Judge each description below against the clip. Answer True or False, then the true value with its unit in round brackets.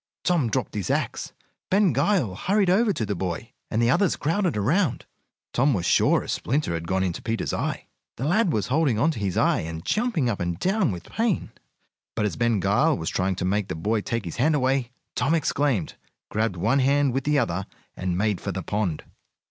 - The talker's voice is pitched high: False (120 Hz)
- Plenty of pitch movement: True (8.0 semitones)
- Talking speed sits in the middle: False (210 wpm)